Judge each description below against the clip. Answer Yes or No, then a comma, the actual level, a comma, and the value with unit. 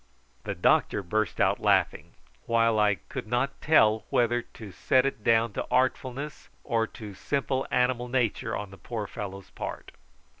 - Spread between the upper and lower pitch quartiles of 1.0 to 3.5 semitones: Yes, average, 3.1 semitones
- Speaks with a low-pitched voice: Yes, low, 115 Hz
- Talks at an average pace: Yes, average, 155 wpm